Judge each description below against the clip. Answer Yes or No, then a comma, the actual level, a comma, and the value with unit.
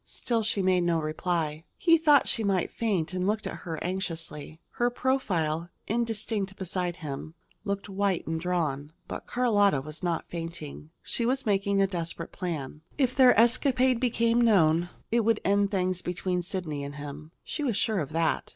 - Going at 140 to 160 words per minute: No, average, 170 wpm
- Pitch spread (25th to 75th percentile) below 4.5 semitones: No, wide, 5.4 semitones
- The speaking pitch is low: No, medium, 185 Hz